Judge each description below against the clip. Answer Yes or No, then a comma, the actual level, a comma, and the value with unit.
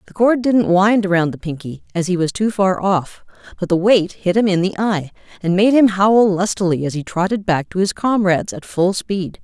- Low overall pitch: No, high, 190 Hz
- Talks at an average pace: No, fast, 230 wpm